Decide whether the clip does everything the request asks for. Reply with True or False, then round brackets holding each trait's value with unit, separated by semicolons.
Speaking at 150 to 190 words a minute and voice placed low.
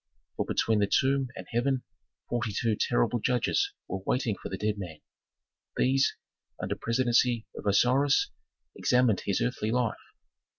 False (140 wpm; 120 Hz)